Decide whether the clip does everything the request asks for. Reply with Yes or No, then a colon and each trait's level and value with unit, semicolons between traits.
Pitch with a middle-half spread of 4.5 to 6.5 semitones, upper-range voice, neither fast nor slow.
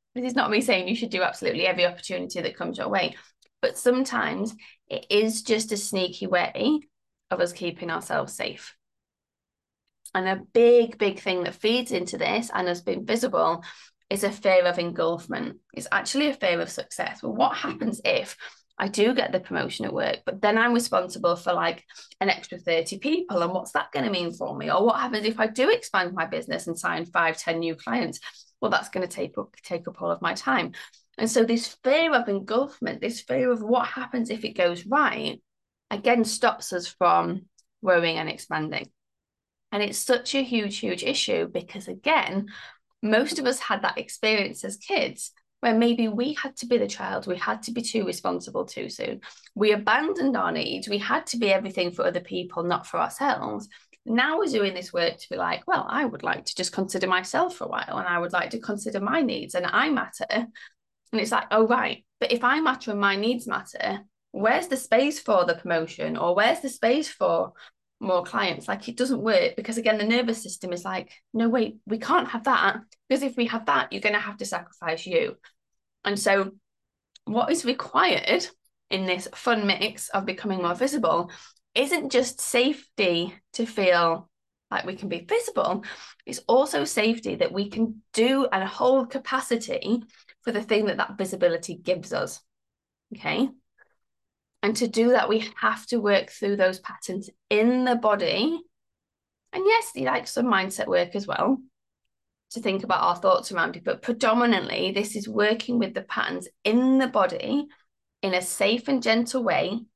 Yes: average, 4.9 semitones; high, 220 Hz; average, 190 wpm